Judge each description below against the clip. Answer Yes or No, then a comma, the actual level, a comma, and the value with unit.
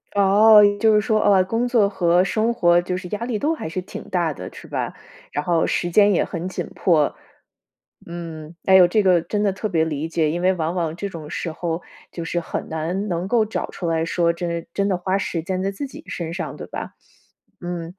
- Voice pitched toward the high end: No, medium, 180 Hz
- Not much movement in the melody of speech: No, average, 3.3 semitones